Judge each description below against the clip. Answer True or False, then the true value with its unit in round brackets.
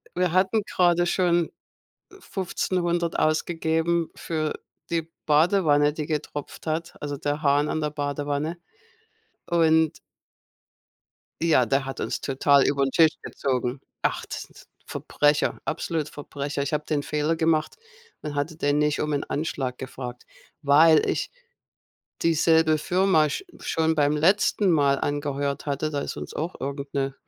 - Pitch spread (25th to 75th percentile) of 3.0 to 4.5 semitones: False (2.5 semitones)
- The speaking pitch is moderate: True (150 Hz)